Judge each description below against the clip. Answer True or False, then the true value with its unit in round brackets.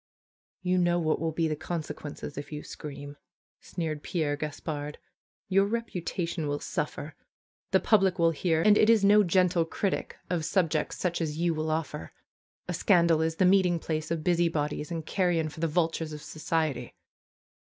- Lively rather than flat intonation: False (2.6 semitones)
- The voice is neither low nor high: True (165 Hz)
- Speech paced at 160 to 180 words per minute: True (170 wpm)